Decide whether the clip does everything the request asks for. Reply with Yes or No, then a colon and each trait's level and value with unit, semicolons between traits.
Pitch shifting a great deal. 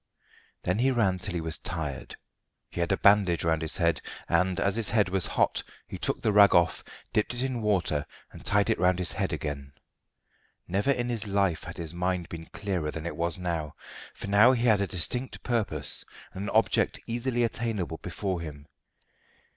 No: average, 4.1 semitones